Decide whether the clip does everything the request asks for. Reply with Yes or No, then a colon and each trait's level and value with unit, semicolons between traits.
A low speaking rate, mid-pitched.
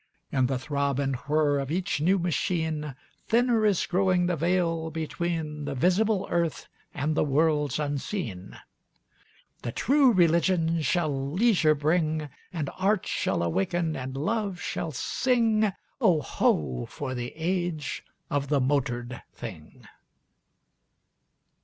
Yes: slow, 125 wpm; medium, 155 Hz